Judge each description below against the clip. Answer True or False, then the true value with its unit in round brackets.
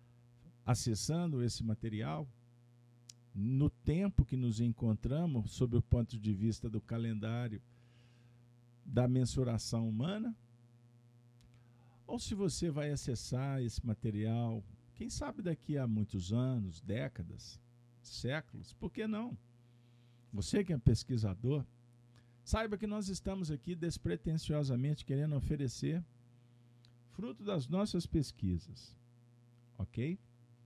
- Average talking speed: False (105 wpm)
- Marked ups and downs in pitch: False (3.0 semitones)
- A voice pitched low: True (120 Hz)